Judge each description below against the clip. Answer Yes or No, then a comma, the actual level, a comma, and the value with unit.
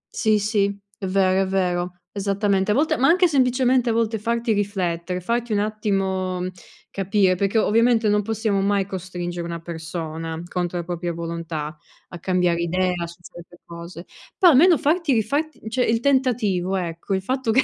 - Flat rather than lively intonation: No, average, 4.4 semitones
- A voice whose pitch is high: Yes, high, 195 Hz